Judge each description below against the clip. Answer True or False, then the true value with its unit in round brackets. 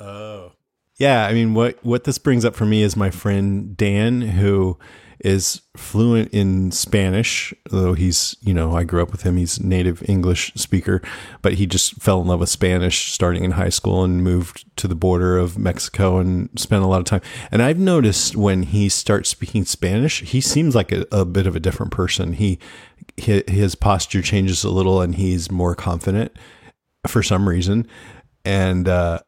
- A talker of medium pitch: False (95 Hz)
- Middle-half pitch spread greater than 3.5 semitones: False (2.9 semitones)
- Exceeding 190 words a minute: False (185 wpm)